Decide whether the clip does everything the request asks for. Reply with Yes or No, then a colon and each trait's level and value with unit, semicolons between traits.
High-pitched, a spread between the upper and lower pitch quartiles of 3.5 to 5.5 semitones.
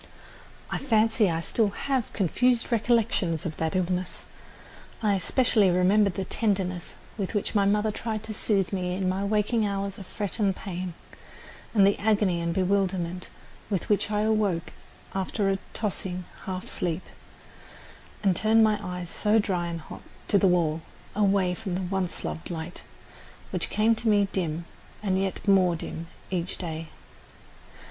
No: high, 195 Hz; average, 2.9 semitones